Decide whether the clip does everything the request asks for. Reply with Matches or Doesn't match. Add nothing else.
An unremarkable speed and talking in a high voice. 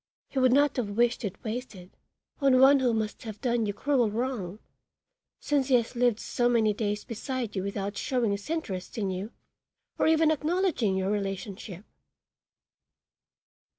Matches